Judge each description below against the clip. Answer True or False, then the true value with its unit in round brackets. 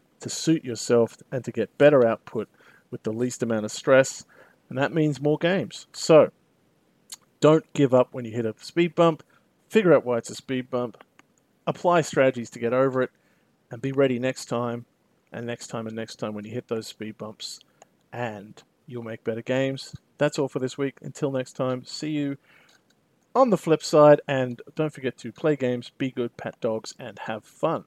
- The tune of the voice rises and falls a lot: False (3.7 semitones)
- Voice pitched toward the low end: True (130 Hz)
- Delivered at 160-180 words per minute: False (195 wpm)